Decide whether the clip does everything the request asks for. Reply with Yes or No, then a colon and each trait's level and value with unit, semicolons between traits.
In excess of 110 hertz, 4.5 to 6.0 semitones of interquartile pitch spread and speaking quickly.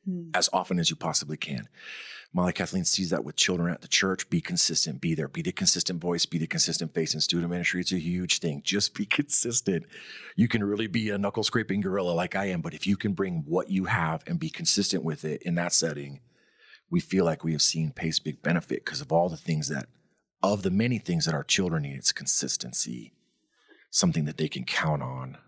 No: very low, 90 Hz; average, 5.0 semitones; fast, 225 wpm